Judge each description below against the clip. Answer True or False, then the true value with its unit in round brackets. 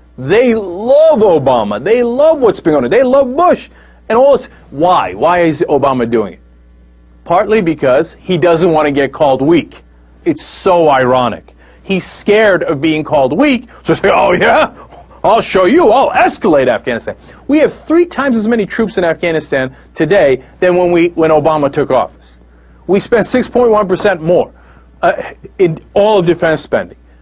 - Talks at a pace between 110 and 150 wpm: False (165 wpm)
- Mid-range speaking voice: True (170 Hz)